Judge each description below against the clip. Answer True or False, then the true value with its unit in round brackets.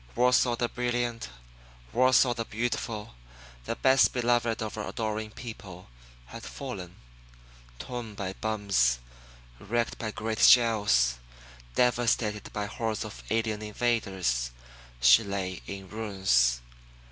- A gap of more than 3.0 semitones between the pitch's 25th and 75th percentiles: True (3.4 semitones)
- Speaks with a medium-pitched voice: False (110 Hz)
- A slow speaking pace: True (110 wpm)